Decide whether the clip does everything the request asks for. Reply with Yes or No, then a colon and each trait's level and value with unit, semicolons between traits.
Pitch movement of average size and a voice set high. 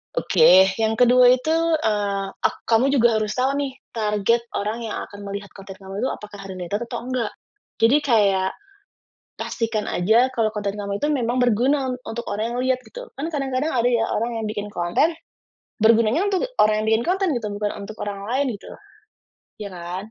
Yes: average, 3.7 semitones; high, 220 Hz